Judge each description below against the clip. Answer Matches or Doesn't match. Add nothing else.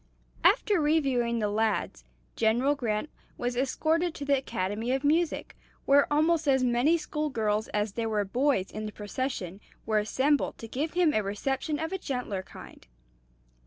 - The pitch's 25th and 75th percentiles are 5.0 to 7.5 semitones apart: Matches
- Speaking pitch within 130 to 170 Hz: Doesn't match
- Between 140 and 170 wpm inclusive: Matches